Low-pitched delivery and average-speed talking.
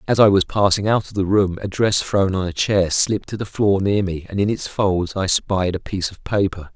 No: very low, 95 Hz; fast, 265 wpm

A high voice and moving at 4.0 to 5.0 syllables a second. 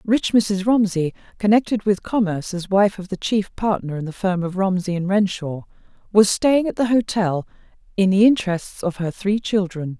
Yes: high, 195 Hz; 4.9 syllables/s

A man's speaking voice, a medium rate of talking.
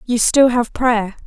No: female; average, 190 wpm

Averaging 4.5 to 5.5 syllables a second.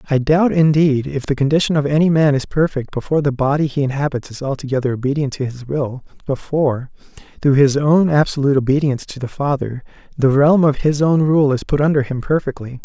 No: 5.9 syllables/s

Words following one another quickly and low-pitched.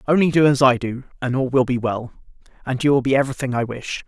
Yes: fast, 265 wpm; low, 130 Hz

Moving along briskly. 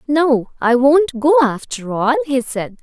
No: average, 170 wpm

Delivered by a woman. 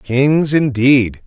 No: male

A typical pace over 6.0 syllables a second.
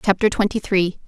No: 5.4 syllables/s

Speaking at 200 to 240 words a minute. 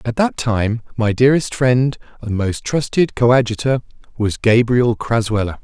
No: average, 140 wpm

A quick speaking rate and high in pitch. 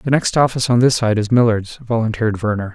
No: fast, 220 wpm; low, 115 Hz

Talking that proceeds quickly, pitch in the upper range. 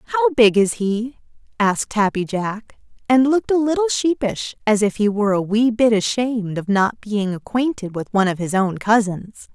No: average, 190 wpm; high, 215 Hz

